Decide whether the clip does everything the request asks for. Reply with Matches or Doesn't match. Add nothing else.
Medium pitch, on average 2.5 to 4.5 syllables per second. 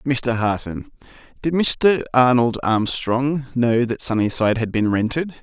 Doesn't match